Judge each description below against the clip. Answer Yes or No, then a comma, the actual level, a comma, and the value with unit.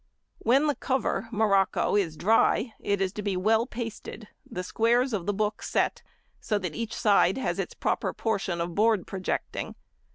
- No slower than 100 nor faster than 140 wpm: No, average, 170 wpm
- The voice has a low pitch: No, high, 210 Hz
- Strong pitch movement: No, average, 2.9 semitones